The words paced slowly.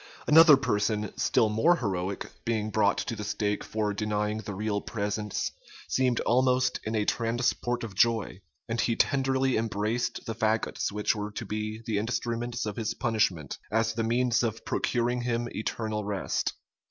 No: average, 160 wpm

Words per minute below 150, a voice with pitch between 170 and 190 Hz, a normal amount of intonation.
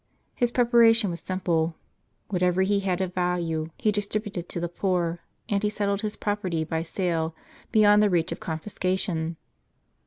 No: average, 155 wpm; medium, 185 Hz; average, 3.4 semitones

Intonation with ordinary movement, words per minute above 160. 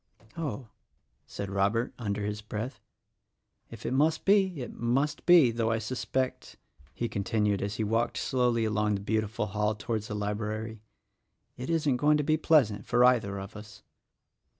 Yes: average, 3.7 semitones; average, 170 wpm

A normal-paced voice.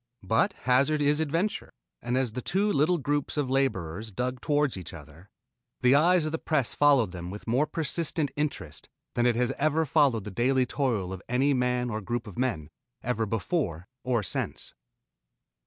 Yes: average, 175 wpm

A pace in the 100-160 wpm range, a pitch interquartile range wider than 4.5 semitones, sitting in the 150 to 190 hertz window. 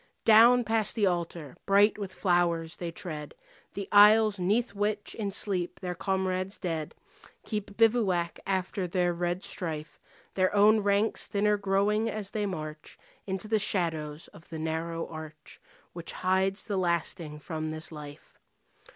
No: average, 145 wpm; average, 3.7 semitones; medium, 185 Hz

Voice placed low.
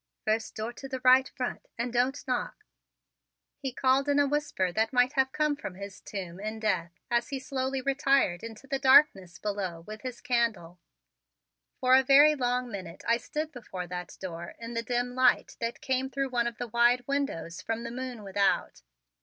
No: high, 245 Hz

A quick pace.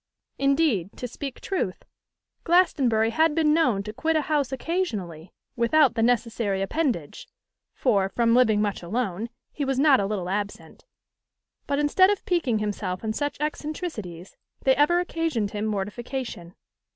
No: average, 145 wpm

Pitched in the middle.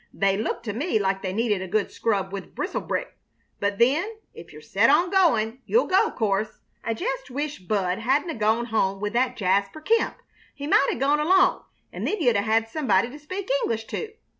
No: high, 230 Hz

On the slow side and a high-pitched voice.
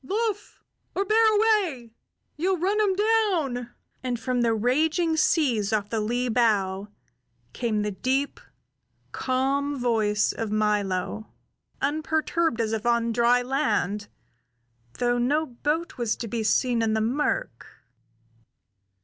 Yes: slow, 125 wpm; high, 245 Hz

